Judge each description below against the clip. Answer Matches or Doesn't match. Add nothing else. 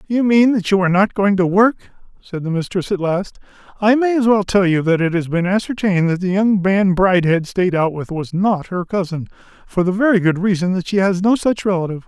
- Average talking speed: Doesn't match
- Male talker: Matches